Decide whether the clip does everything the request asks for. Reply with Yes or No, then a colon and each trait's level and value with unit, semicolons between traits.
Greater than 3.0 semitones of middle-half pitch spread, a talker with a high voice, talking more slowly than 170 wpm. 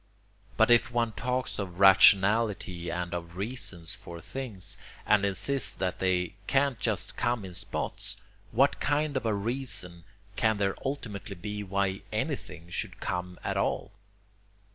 No: average, 4.7 semitones; low, 100 Hz; average, 140 wpm